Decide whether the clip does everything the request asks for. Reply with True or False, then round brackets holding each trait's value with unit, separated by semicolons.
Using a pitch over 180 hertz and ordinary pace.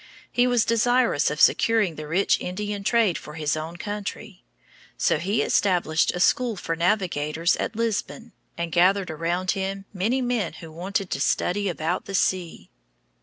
True (190 Hz; 160 wpm)